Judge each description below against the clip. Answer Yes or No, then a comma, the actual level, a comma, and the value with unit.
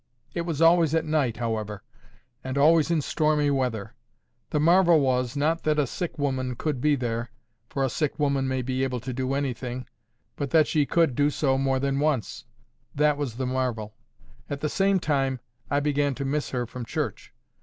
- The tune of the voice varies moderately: Yes, average, 3.2 semitones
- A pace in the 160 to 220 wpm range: Yes, average, 185 wpm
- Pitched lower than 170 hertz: Yes, low, 135 Hz